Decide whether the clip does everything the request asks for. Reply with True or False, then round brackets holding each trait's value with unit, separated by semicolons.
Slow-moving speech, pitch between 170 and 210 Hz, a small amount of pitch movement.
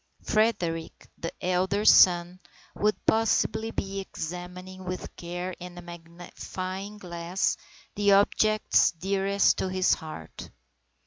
True (110 wpm; 185 Hz; 2.3 semitones)